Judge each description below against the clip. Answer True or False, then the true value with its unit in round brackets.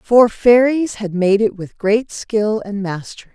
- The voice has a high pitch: True (215 Hz)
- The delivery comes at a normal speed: True (180 wpm)